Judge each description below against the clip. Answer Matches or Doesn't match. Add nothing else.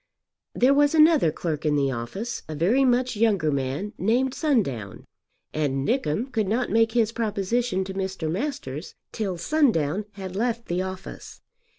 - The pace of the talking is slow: Doesn't match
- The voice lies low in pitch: Doesn't match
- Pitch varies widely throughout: Matches